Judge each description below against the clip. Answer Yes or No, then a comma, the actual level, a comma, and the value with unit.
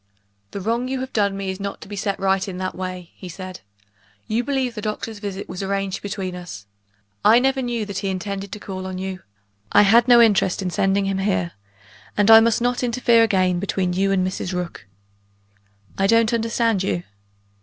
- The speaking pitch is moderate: No, high, 195 Hz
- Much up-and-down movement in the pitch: No, average, 3.3 semitones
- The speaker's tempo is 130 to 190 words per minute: No, average, 200 wpm